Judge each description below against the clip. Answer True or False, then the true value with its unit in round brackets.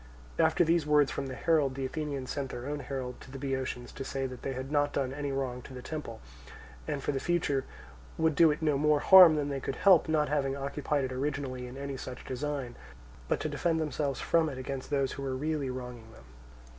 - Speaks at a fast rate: True (225 wpm)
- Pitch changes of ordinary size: False (2.3 semitones)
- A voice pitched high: False (140 Hz)